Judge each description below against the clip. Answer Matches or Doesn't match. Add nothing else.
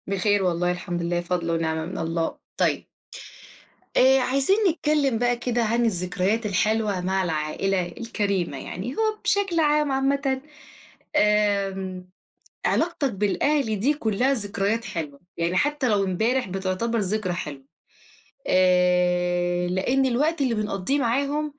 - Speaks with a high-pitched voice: Matches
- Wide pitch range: Matches